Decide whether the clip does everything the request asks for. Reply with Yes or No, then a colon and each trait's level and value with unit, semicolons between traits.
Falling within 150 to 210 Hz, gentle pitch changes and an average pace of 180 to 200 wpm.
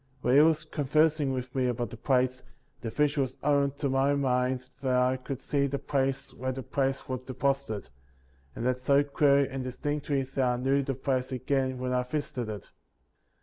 No: low, 135 Hz; narrow, 1.7 semitones; average, 190 wpm